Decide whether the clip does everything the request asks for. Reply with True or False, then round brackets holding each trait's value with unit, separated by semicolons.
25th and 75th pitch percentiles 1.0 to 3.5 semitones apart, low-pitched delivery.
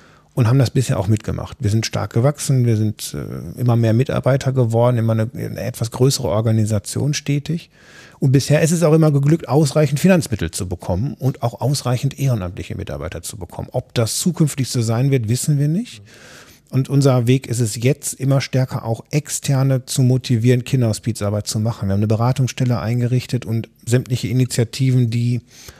True (3.1 semitones; 125 Hz)